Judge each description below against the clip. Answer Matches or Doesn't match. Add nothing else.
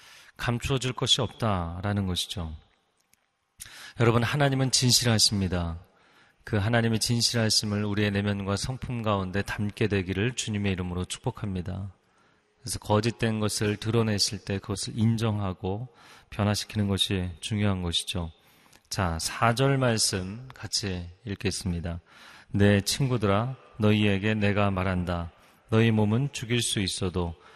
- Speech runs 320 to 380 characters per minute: Doesn't match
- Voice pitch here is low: Matches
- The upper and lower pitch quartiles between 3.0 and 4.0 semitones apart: Matches